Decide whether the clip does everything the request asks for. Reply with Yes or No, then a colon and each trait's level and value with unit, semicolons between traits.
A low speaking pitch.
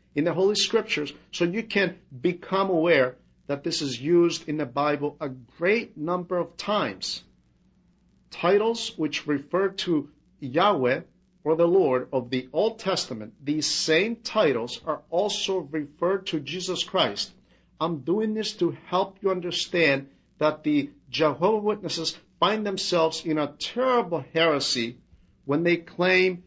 No: medium, 165 Hz